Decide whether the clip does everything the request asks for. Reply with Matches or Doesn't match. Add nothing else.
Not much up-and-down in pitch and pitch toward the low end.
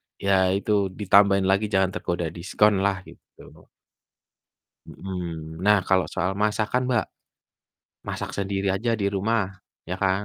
Matches